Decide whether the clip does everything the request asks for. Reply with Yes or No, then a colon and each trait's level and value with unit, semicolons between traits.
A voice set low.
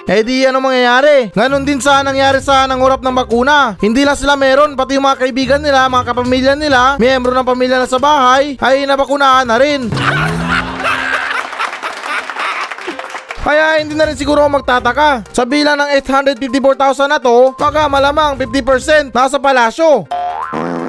No: very high, 270 Hz